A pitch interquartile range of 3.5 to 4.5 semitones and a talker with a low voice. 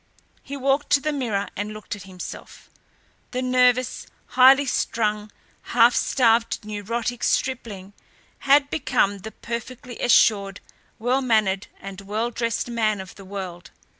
No: average, 3.8 semitones; high, 230 Hz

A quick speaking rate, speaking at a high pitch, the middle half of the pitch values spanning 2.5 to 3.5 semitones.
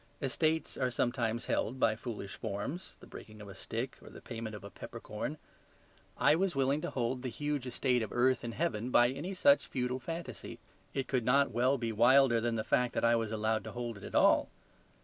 No: fast, 210 wpm; low, 125 Hz; average, 3.1 semitones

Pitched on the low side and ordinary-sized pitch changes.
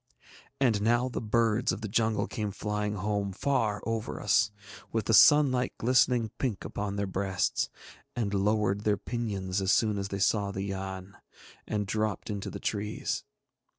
No: low, 105 Hz; narrow, 2.3 semitones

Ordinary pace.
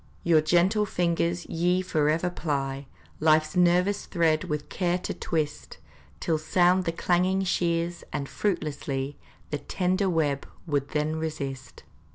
No: slow, 130 wpm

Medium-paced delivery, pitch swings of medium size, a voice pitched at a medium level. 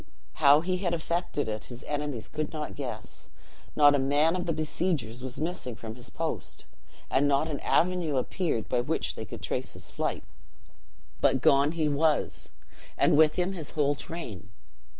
Yes: average, 170 wpm; average, 3.7 semitones; medium, 150 Hz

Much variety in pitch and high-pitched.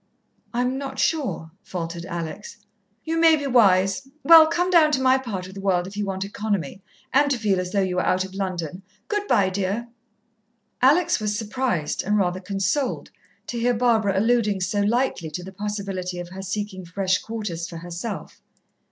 No: average, 4.9 semitones; high, 200 Hz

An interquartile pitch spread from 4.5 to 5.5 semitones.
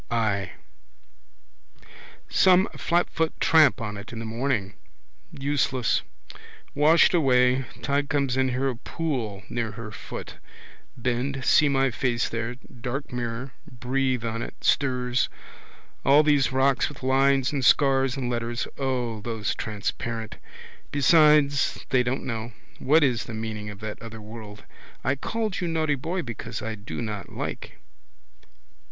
No: average, 3.4 semitones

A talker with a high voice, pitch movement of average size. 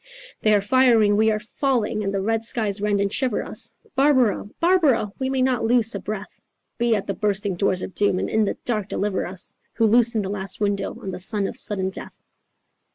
Yes: high, 210 Hz; average, 3.0 semitones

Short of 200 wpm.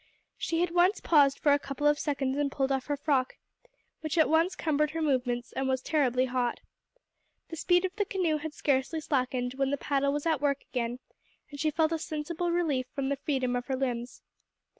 No: fast, 205 wpm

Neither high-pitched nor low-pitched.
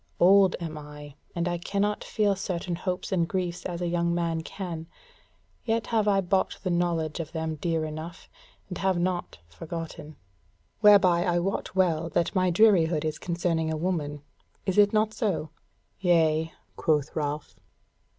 Yes: medium, 175 Hz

